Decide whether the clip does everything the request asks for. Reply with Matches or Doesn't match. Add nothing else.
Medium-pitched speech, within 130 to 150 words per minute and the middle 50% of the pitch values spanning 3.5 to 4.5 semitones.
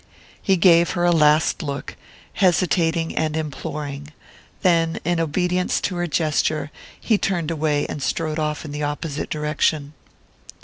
Doesn't match